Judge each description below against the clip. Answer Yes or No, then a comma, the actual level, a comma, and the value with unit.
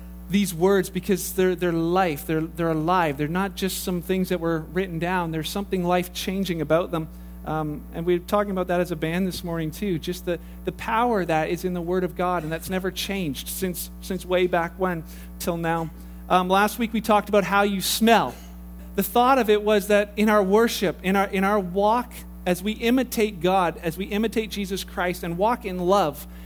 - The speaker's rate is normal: No, fast, 215 wpm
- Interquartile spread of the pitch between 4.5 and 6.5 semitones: No, average, 3.4 semitones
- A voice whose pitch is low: No, medium, 185 Hz